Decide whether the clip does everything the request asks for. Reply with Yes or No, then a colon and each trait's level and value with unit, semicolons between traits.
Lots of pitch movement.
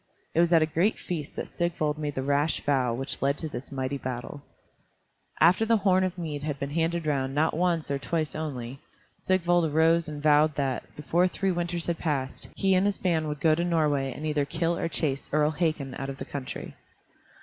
No: average, 3.4 semitones